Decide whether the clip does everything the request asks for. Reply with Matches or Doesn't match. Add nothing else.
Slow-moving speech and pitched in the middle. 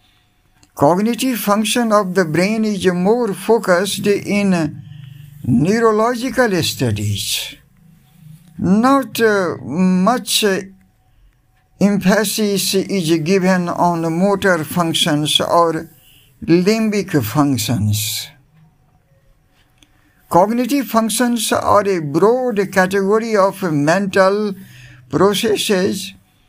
Matches